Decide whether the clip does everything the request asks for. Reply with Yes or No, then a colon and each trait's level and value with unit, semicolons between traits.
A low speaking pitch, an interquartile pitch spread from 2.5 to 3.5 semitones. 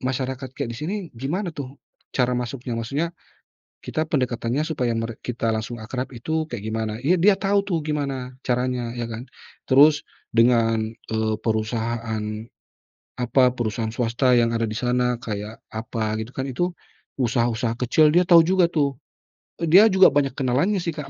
No: low, 125 Hz; average, 4.3 semitones